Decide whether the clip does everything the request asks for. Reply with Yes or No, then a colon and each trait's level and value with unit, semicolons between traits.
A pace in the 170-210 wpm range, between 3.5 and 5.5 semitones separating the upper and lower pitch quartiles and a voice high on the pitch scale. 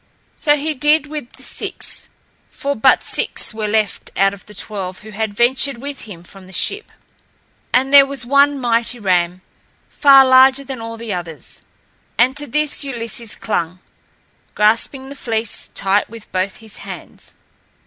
No: average, 160 wpm; average, 5.0 semitones; high, 230 Hz